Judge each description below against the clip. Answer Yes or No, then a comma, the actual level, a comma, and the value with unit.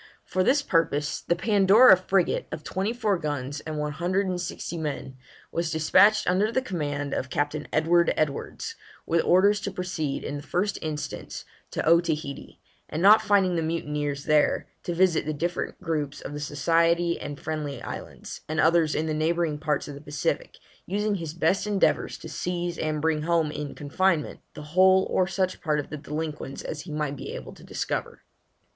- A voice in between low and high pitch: Yes, medium, 165 Hz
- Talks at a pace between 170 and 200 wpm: Yes, average, 180 wpm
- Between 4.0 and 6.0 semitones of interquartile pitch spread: No, average, 3.6 semitones